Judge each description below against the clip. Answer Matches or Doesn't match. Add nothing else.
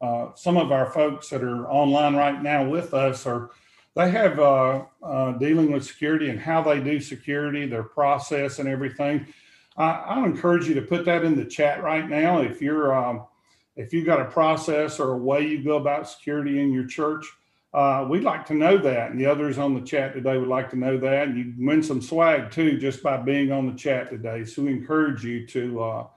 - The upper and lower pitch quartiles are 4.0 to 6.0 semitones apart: Doesn't match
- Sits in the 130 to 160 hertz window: Matches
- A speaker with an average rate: Doesn't match